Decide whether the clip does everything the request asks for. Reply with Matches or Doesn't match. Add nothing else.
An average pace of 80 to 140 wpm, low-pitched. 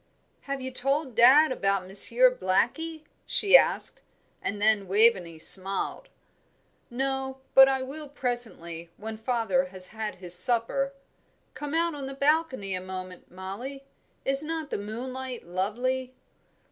Doesn't match